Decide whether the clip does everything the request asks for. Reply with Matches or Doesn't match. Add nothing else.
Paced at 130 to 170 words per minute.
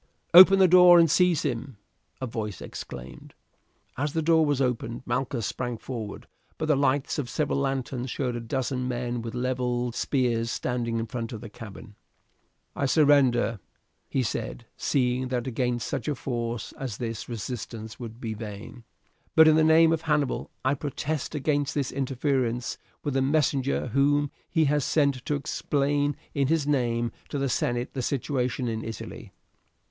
Matches